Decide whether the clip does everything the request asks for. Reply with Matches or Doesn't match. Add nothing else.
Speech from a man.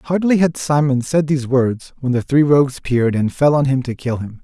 Matches